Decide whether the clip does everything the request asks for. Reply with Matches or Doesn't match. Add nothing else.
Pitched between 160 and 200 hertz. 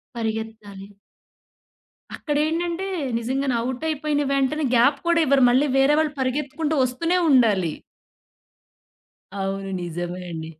Doesn't match